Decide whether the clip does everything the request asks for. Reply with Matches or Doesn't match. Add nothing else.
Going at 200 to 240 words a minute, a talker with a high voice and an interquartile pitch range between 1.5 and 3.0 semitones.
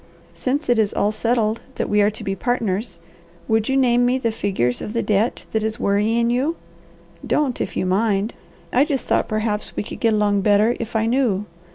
Matches